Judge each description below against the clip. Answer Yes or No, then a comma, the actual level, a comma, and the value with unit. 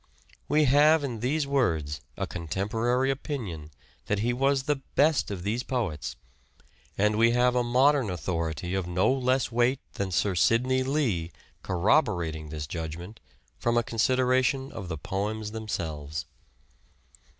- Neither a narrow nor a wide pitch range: No, wide, 6.9 semitones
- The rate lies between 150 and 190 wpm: No, average, 140 wpm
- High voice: No, low, 115 Hz